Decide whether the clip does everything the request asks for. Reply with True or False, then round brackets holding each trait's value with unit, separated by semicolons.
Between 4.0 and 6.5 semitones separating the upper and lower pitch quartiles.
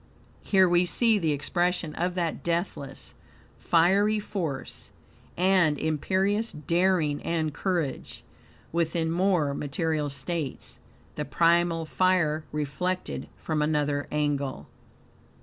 False (3.4 semitones)